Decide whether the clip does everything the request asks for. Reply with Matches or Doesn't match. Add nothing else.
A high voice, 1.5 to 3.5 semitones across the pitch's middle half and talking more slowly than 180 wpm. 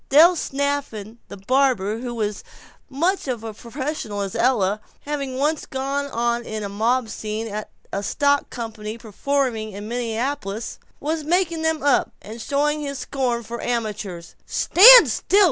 Doesn't match